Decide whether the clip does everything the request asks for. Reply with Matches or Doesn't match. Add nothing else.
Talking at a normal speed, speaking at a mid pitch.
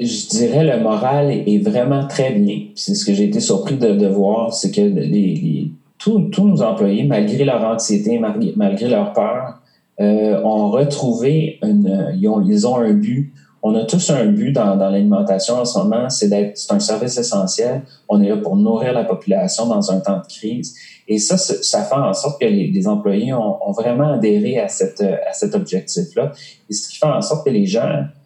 Doesn't match